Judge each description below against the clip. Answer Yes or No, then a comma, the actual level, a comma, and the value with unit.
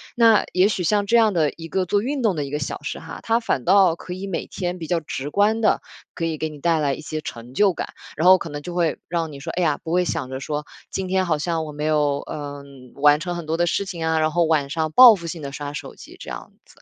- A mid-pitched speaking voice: Yes, medium, 165 Hz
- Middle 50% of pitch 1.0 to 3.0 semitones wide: No, average, 3.8 semitones